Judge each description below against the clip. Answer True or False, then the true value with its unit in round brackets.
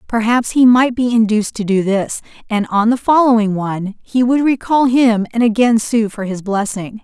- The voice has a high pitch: True (225 Hz)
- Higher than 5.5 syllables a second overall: False (4.9 syllables/s)